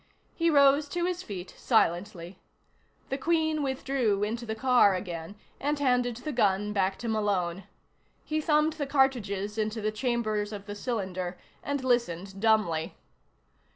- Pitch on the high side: Yes, high, 220 Hz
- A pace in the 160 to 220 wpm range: No, average, 145 wpm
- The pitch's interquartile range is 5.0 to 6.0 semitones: Yes, wide, 5.4 semitones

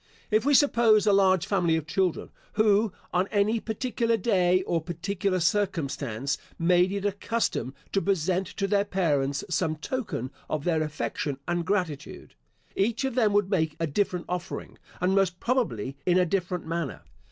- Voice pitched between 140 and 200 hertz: Yes, medium, 185 Hz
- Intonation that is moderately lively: Yes, average, 3.7 semitones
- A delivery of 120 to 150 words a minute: No, average, 165 wpm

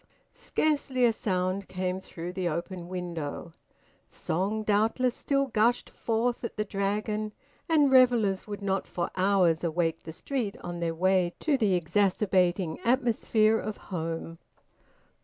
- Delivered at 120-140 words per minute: Yes, slow, 135 wpm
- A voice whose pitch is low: No, high, 195 Hz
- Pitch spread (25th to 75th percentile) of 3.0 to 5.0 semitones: Yes, average, 4.1 semitones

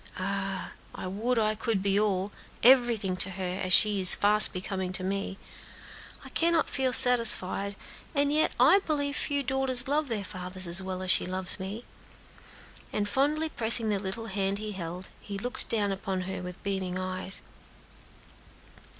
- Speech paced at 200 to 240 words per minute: No, average, 165 wpm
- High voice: Yes, high, 200 Hz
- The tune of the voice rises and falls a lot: No, average, 4.5 semitones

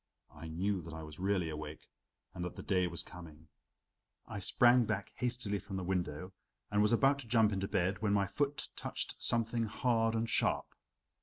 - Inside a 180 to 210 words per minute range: Yes, average, 185 wpm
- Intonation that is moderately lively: Yes, average, 4.4 semitones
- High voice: No, low, 100 Hz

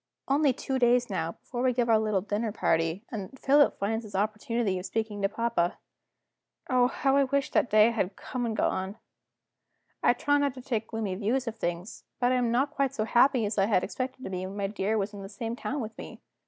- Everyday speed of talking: No, fast, 225 wpm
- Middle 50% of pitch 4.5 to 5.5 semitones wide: No, average, 3.9 semitones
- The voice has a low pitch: No, high, 225 Hz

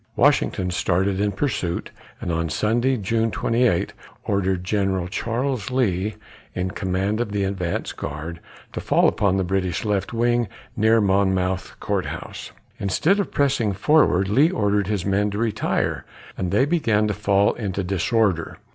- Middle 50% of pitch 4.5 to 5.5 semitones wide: No, average, 3.4 semitones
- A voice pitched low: Yes, low, 100 Hz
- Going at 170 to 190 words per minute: No, average, 150 wpm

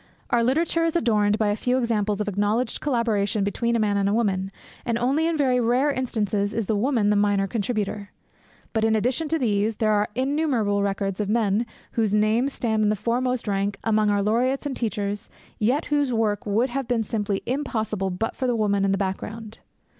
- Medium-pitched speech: No, high, 220 Hz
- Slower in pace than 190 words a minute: No, average, 200 wpm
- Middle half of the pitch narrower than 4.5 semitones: Yes, average, 3.2 semitones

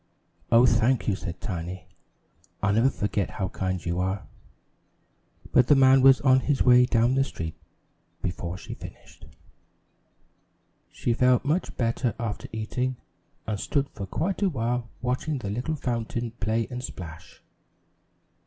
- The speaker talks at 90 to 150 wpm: Yes, average, 145 wpm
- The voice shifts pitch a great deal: No, average, 4.6 semitones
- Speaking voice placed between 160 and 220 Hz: No, low, 120 Hz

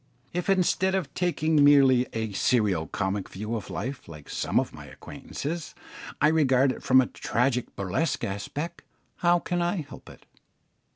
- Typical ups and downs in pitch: No, wide, 7.2 semitones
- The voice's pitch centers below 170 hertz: Yes, low, 135 Hz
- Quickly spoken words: No, average, 160 wpm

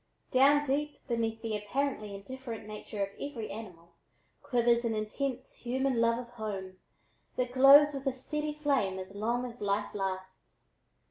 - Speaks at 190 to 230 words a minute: No, average, 150 wpm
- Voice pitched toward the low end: No, high, 235 Hz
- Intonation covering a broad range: No, average, 4.3 semitones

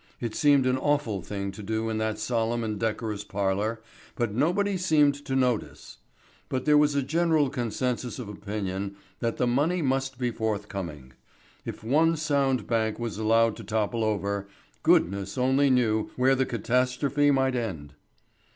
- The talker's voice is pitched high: No, low, 120 Hz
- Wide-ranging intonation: No, average, 4.1 semitones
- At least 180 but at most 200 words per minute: No, average, 160 wpm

